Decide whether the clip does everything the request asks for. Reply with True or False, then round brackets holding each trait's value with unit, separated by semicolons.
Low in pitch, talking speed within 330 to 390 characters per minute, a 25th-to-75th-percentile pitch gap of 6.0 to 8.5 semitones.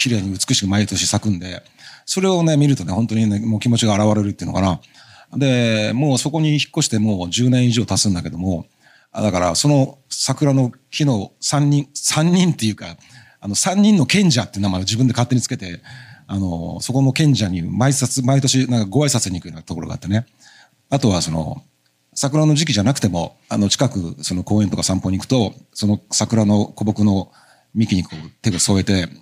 False (115 Hz; 365 characters per minute; 5.6 semitones)